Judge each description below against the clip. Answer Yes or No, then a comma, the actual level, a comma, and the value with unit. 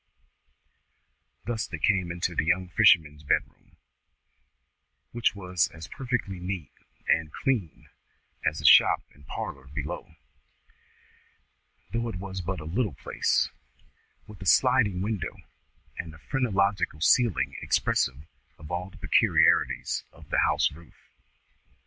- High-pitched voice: No, very low, 90 Hz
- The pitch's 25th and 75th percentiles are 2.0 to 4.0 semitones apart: No, average, 4.6 semitones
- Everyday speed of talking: No, slow, 125 wpm